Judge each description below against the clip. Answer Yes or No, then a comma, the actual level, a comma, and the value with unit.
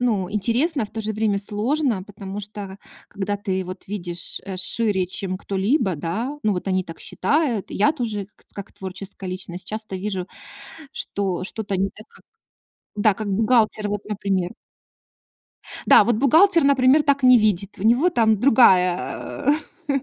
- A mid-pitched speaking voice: No, high, 205 Hz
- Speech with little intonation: No, average, 3.6 semitones